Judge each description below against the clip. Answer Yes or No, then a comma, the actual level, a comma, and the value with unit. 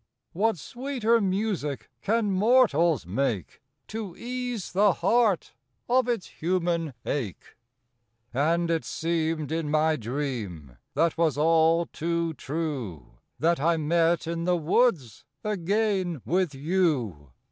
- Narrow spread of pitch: No, average, 4.8 semitones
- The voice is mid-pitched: Yes, medium, 165 Hz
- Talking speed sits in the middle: No, slow, 120 wpm